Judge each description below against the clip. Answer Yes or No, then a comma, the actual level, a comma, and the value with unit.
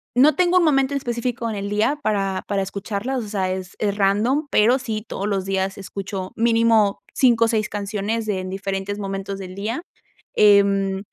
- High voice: Yes, high, 205 Hz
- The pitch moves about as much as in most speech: Yes, average, 3.0 semitones